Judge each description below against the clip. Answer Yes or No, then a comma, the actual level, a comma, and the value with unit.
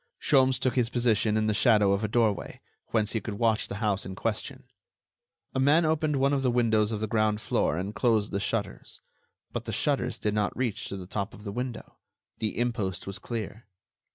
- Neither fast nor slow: No, fast, 210 wpm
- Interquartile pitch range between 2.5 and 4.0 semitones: Yes, average, 2.9 semitones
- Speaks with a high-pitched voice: No, low, 110 Hz